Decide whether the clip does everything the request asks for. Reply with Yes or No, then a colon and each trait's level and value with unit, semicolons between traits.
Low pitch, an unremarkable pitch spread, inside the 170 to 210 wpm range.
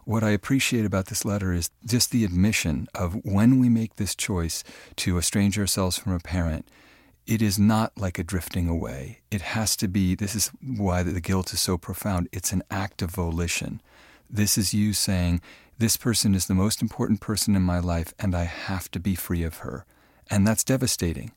Yes: very low, 95 Hz; average, 3.4 semitones; average, 200 wpm